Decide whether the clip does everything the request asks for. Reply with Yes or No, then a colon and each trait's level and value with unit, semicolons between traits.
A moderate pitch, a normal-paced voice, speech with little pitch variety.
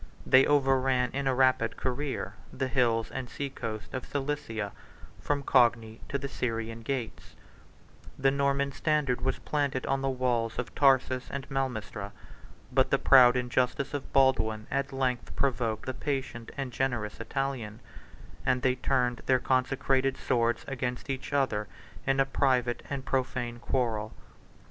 No: low, 130 Hz; average, 150 wpm; narrow, 2.2 semitones